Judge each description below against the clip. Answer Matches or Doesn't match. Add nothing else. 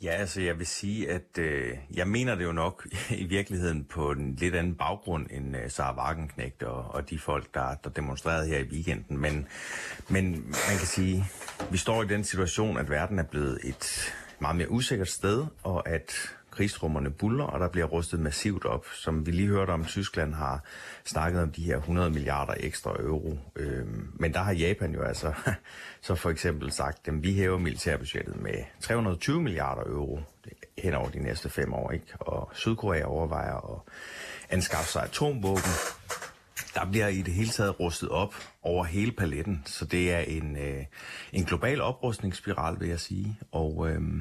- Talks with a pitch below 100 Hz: Matches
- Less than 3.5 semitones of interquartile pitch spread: Doesn't match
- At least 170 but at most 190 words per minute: Matches